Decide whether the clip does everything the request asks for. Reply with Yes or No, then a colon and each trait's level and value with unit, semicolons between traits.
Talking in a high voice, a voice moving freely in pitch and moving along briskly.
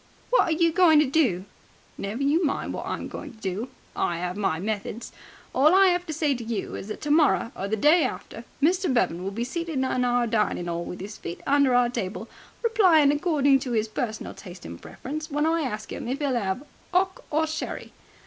Yes: very high, 260 Hz; wide, 6.7 semitones; fast, 215 wpm